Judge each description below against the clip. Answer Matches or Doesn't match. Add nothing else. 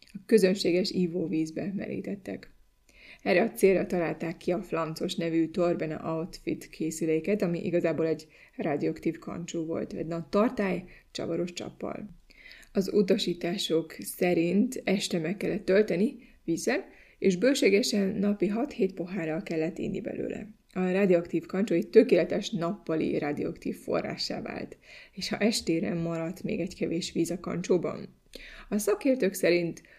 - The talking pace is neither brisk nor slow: Matches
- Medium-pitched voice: Matches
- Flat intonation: Doesn't match